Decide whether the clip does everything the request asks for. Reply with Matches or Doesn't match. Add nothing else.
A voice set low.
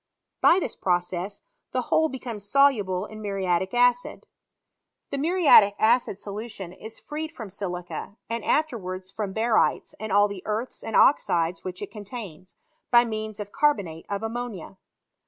Doesn't match